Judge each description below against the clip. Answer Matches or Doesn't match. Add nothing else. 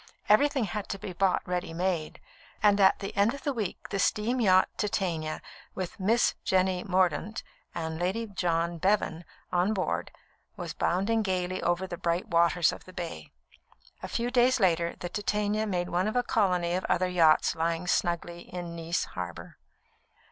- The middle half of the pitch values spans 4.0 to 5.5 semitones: Doesn't match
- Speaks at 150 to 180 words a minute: Matches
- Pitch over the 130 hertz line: Matches